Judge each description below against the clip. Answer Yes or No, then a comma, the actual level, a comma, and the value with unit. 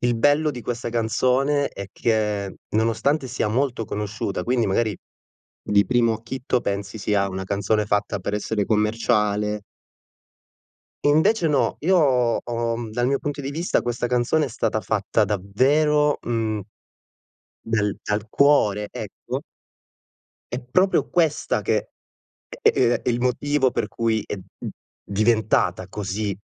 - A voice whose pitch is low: Yes, low, 115 Hz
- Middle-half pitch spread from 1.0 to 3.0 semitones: No, average, 3.8 semitones